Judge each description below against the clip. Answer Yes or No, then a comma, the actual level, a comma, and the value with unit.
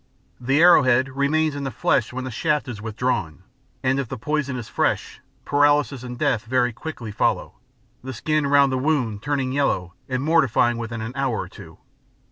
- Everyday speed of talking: Yes, average, 185 wpm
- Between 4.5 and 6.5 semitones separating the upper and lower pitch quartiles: No, average, 3.1 semitones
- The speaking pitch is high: No, low, 130 Hz